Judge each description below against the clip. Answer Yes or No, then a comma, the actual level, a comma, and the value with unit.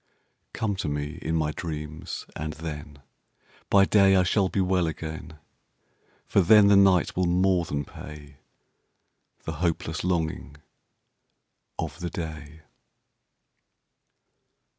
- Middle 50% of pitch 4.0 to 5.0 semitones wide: No, average, 3.2 semitones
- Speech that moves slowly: Yes, slow, 105 wpm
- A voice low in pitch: Yes, very low, 80 Hz